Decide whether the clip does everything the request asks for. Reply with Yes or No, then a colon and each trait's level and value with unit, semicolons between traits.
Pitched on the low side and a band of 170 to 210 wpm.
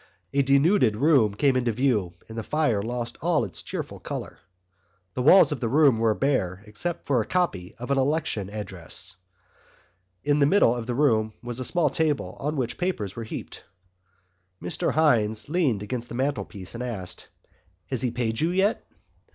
Yes: low, 125 Hz; average, 175 wpm